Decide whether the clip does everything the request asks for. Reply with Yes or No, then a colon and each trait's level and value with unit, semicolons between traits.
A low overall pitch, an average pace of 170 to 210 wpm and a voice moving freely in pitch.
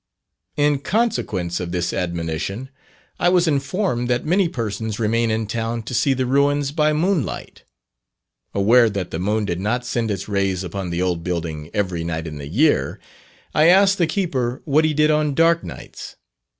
Yes: low, 115 Hz; average, 175 wpm; wide, 8.4 semitones